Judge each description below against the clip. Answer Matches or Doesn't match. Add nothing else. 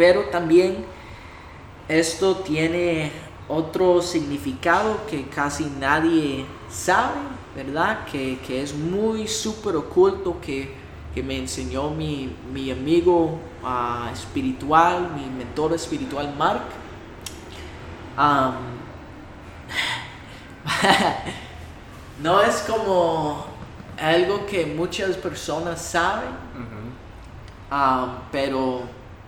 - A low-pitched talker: Doesn't match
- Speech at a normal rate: Doesn't match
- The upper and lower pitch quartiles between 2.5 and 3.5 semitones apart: Doesn't match